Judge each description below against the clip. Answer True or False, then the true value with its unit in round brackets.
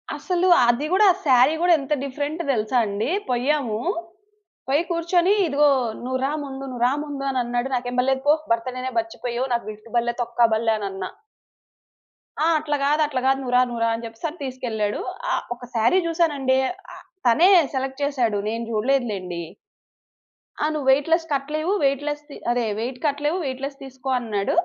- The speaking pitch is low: False (265 Hz)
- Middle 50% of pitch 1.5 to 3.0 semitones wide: False (3.7 semitones)